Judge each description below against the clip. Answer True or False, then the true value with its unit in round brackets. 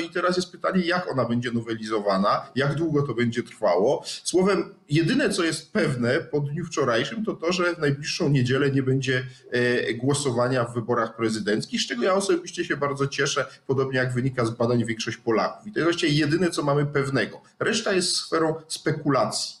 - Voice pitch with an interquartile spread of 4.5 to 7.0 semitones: True (5.6 semitones)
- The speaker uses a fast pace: True (185 wpm)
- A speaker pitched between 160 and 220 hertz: False (140 Hz)